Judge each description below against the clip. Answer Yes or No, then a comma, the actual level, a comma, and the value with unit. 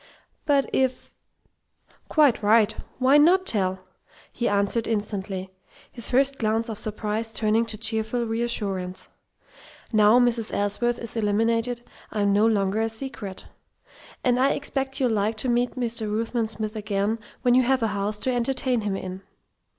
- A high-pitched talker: Yes, high, 225 Hz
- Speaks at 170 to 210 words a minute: No, average, 150 wpm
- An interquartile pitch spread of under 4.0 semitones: Yes, average, 2.8 semitones